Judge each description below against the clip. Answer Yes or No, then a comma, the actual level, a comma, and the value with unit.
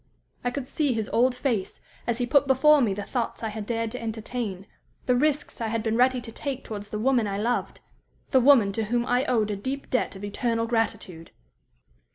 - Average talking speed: No, fast, 210 wpm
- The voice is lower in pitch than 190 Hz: No, high, 235 Hz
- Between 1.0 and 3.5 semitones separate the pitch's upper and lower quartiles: Yes, average, 2.8 semitones